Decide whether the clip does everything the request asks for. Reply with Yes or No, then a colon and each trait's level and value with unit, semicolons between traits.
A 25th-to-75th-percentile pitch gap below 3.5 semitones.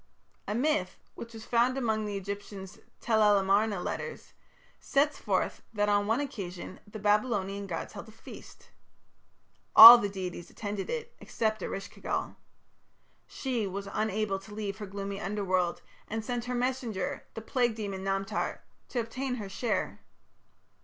Yes: average, 2.9 semitones